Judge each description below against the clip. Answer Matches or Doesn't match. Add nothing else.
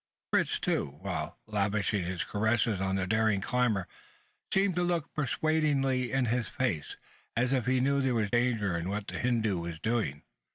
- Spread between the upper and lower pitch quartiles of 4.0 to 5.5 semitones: Matches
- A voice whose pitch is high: Doesn't match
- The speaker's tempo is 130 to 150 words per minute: Doesn't match